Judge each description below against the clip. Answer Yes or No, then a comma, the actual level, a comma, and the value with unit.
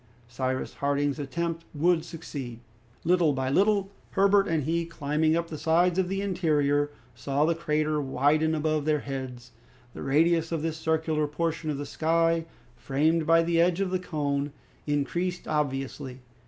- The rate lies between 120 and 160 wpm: Yes, average, 155 wpm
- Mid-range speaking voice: Yes, medium, 155 Hz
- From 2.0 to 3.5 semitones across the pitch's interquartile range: Yes, average, 2.8 semitones